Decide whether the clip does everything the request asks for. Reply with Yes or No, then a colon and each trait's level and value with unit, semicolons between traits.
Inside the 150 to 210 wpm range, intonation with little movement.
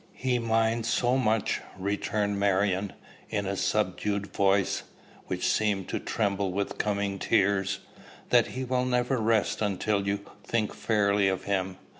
No: average, 140 wpm; narrow, 2.3 semitones